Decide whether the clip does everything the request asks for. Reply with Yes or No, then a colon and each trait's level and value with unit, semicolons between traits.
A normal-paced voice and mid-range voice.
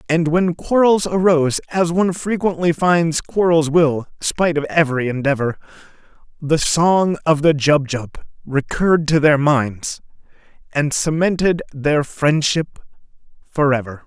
No: slow, 120 wpm; medium, 155 Hz